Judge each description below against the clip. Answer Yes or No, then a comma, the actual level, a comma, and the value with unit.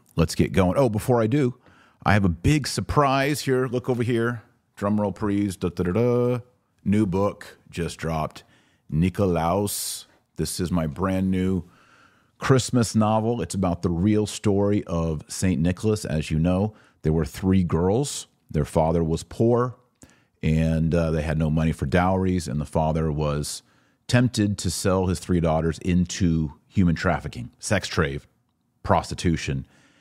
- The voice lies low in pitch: Yes, very low, 95 Hz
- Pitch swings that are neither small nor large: No, wide, 5.8 semitones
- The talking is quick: No, average, 155 wpm